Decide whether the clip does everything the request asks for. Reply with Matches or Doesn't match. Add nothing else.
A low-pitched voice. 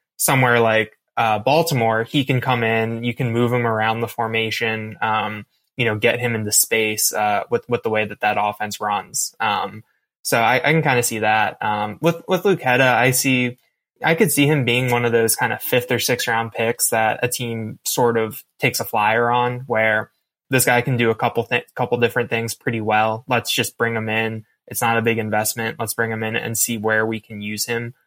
Matches